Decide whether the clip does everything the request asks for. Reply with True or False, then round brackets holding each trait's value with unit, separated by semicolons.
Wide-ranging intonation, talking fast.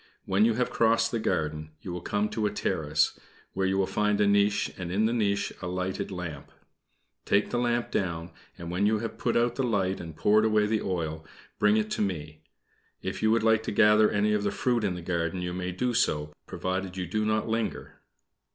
False (3.4 semitones; 220 wpm)